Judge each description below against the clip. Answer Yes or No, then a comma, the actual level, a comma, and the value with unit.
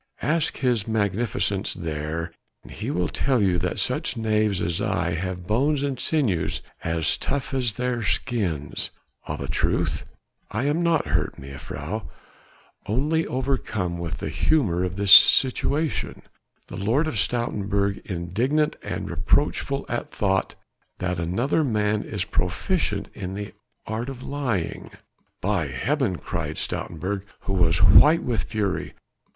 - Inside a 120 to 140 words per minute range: Yes, slow, 135 wpm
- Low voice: Yes, low, 105 Hz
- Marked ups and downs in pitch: Yes, wide, 6.1 semitones